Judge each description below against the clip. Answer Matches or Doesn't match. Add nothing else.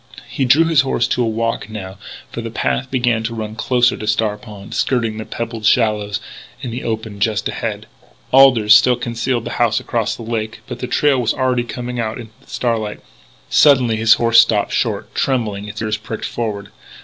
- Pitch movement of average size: Doesn't match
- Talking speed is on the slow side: Doesn't match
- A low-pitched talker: Matches